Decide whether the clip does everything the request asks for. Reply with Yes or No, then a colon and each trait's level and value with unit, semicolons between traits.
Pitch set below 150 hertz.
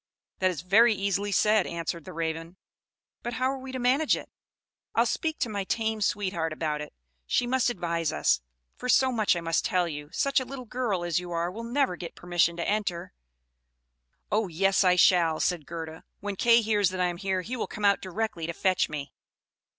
No: high, 190 Hz